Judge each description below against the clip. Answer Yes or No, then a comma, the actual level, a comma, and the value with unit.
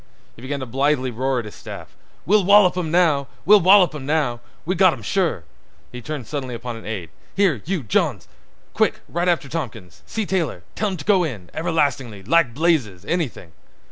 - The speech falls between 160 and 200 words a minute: No, average, 150 wpm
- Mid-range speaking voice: Yes, medium, 145 Hz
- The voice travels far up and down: Yes, wide, 6.8 semitones